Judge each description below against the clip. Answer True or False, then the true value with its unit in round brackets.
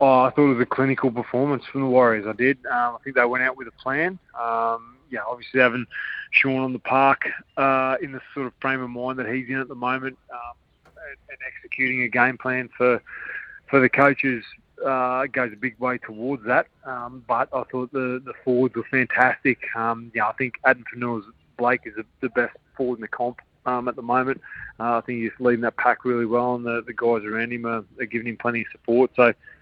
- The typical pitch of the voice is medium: False (125 Hz)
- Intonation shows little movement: True (1.6 semitones)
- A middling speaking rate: False (230 wpm)